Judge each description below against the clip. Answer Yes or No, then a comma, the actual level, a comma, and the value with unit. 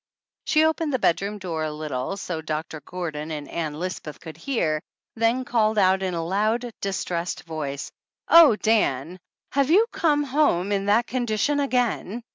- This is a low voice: No, high, 195 Hz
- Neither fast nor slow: Yes, average, 170 wpm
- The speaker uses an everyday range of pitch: No, wide, 7.2 semitones